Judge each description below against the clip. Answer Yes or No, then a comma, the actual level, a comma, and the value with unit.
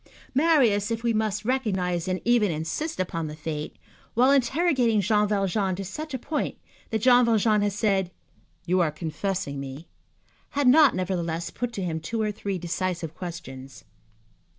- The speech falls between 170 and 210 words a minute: No, average, 160 wpm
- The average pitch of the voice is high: Yes, high, 200 Hz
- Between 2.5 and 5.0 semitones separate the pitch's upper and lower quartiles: No, wide, 5.4 semitones